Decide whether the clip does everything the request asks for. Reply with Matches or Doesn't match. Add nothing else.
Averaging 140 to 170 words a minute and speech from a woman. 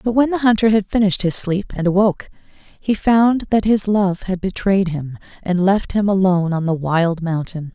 Doesn't match